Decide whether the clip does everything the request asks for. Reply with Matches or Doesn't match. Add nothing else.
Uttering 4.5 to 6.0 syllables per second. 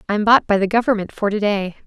Doesn't match